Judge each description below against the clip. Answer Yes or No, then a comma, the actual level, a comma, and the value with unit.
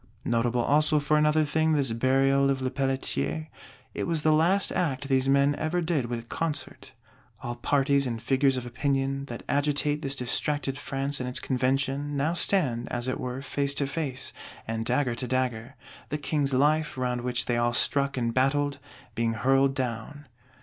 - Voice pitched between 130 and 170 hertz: Yes, low, 135 Hz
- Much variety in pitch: No, narrow, 2.6 semitones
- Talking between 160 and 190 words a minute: Yes, average, 170 wpm